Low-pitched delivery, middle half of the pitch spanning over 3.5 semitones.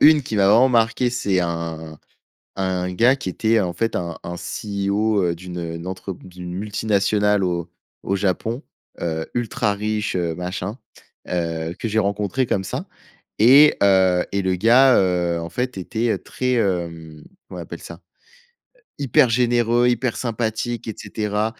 Yes: low, 100 Hz; average, 4.3 semitones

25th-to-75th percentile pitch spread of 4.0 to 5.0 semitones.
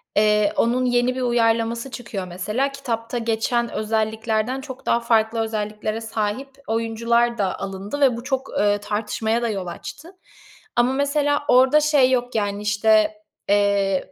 No: average, 3.0 semitones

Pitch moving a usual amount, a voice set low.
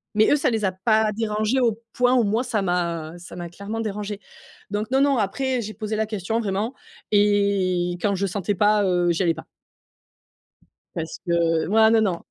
No: average, 3.3 semitones; high, 205 Hz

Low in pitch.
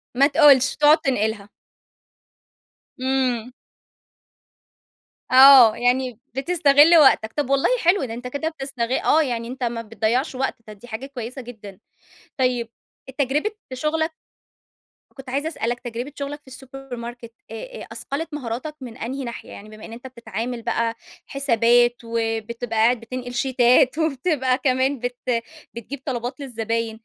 No: very high, 255 Hz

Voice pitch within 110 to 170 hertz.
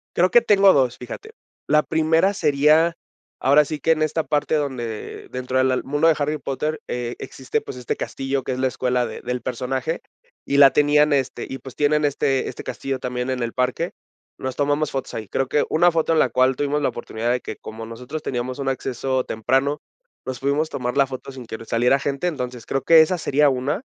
Yes: low, 135 Hz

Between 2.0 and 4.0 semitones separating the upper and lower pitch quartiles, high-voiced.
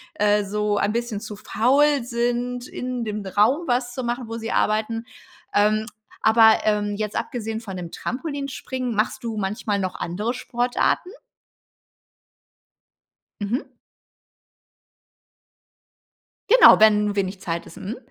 Yes: average, 2.8 semitones; high, 220 Hz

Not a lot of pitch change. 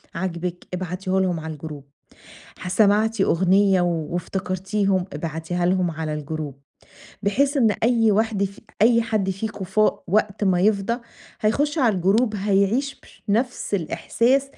No: average, 3.7 semitones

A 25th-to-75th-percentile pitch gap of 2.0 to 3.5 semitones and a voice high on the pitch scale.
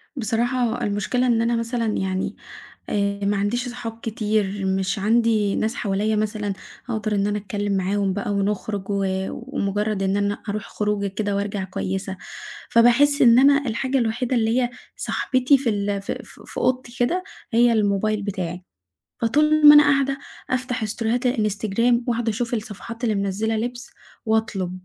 Yes: average, 3.1 semitones; high, 220 Hz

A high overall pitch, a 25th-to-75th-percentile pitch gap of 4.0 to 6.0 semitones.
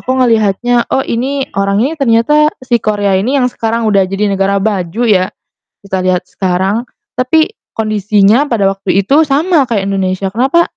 Yes: high, 215 Hz; average, 4.5 semitones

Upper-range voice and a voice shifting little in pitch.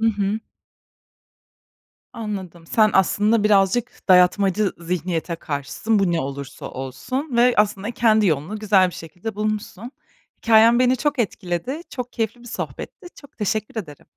No: high, 210 Hz; average, 4.2 semitones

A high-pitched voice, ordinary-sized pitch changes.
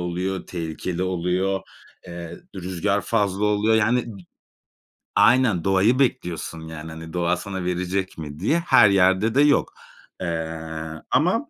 No: very low, 95 Hz; average, 3.4 semitones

